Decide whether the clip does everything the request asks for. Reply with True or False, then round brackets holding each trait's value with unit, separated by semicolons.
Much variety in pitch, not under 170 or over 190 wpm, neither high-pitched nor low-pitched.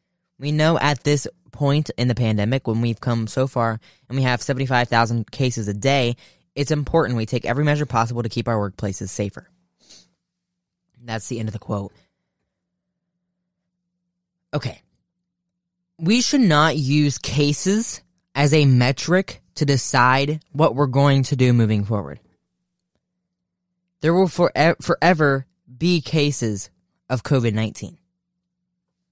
False (6.9 semitones; 135 wpm; 145 Hz)